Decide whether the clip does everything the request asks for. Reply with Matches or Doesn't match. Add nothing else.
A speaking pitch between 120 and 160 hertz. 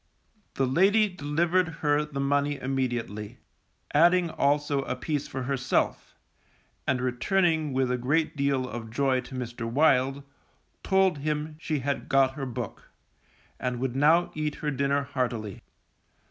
Matches